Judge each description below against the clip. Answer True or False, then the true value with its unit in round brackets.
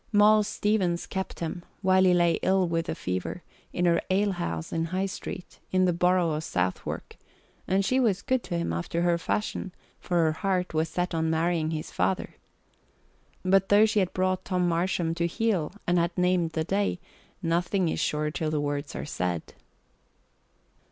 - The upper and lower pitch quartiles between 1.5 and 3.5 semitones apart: True (2.6 semitones)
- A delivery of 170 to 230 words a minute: True (180 wpm)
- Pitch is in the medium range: True (175 Hz)